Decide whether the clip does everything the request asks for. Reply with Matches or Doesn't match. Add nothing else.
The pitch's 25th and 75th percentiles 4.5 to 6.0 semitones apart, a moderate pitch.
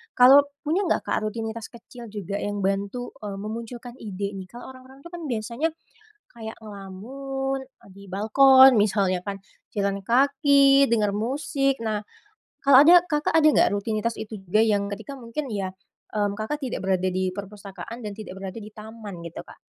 Doesn't match